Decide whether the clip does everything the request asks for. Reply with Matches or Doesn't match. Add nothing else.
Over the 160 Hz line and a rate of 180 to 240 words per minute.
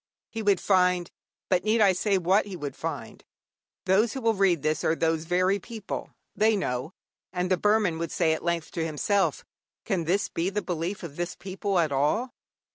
Matches